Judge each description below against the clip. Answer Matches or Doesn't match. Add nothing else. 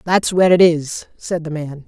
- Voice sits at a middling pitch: Matches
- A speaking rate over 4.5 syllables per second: Matches